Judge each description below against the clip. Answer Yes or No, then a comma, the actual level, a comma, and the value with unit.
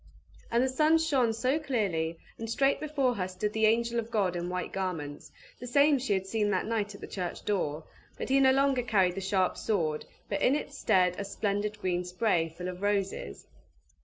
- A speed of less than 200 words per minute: No, fast, 205 wpm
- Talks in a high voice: Yes, high, 210 Hz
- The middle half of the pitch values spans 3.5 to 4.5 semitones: No, average, 5.2 semitones